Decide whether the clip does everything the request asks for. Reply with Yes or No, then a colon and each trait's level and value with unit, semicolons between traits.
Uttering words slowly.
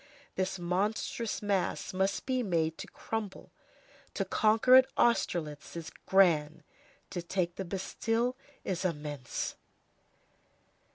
Yes: slow, 110 wpm